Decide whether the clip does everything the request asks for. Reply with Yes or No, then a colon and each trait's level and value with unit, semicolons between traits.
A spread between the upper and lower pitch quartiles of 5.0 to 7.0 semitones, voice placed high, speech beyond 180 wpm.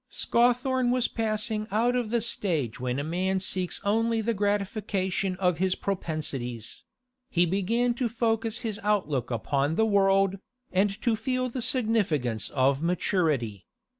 No: wide, 5.5 semitones; high, 200 Hz; average, 140 wpm